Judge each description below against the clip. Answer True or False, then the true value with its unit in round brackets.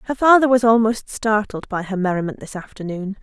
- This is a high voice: True (215 Hz)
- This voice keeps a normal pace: True (185 wpm)